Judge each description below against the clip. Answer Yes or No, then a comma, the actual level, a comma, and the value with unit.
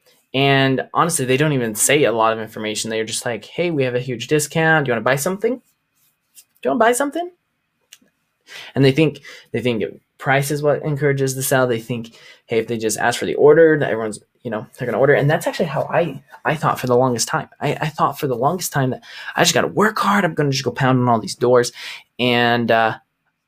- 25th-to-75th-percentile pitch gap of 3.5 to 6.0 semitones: Yes, average, 4.4 semitones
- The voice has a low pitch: Yes, low, 130 Hz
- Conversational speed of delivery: No, fast, 240 wpm